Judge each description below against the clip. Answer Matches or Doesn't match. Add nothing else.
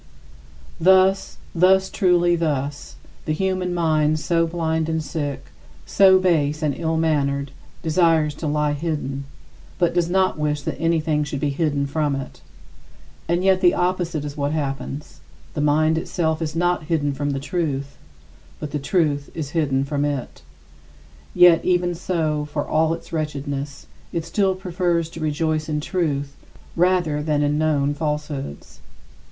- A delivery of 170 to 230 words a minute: Doesn't match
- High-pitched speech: Doesn't match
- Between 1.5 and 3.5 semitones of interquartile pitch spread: Matches